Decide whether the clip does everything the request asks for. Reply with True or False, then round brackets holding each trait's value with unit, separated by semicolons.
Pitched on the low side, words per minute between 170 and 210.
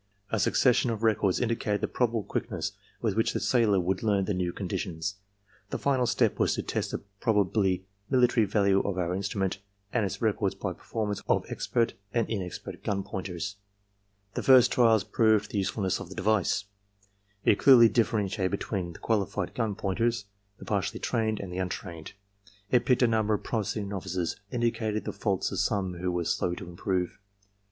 True (100 Hz; 180 wpm)